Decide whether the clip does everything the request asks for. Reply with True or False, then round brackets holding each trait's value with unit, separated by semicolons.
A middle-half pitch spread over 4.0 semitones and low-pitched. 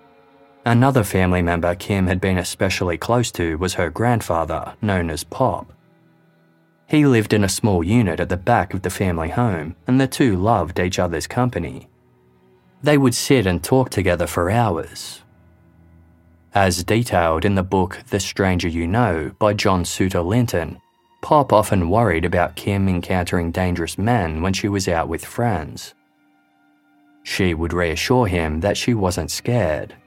True (4.5 semitones; 95 Hz)